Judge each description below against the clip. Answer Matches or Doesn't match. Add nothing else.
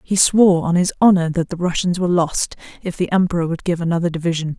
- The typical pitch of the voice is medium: Matches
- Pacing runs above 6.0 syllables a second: Matches